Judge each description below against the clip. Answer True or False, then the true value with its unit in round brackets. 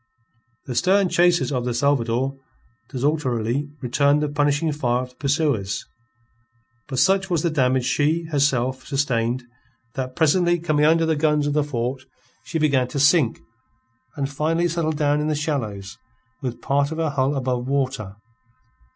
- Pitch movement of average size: True (3.2 semitones)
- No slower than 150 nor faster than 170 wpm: True (155 wpm)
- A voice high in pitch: False (145 Hz)